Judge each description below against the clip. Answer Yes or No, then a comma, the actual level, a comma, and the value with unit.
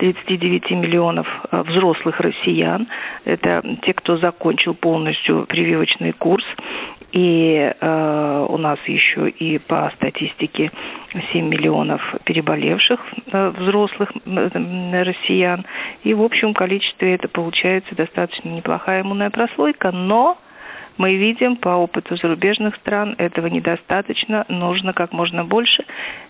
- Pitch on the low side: No, medium, 180 Hz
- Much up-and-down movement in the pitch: No, average, 3.4 semitones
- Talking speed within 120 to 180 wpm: No, slow, 110 wpm